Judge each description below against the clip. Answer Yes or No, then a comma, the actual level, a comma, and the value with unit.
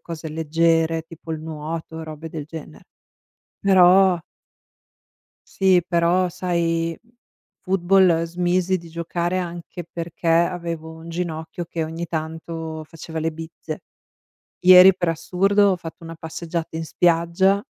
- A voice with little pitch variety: Yes, narrow, 1.6 semitones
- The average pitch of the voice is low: No, medium, 165 Hz